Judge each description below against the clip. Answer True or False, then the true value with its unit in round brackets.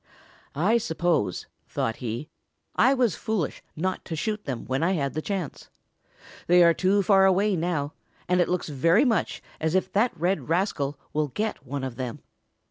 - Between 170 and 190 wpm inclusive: True (175 wpm)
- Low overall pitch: False (175 Hz)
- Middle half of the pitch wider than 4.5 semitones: True (5.2 semitones)